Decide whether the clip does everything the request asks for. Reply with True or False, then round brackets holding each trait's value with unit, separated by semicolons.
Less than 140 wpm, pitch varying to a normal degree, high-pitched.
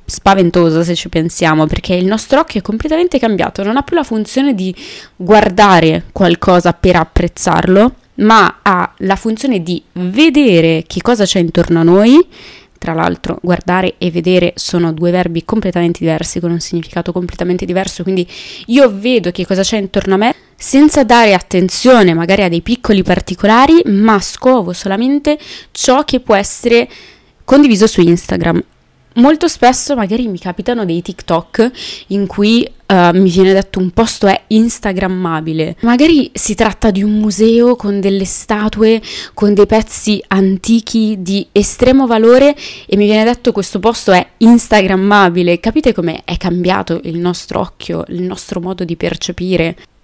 False (155 wpm; 4.3 semitones; 195 Hz)